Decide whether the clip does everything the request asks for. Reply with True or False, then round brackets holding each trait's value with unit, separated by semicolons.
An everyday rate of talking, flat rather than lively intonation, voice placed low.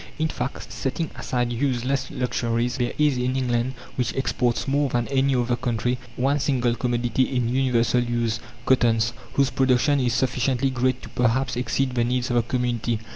True (170 wpm; 1.7 semitones; 125 Hz)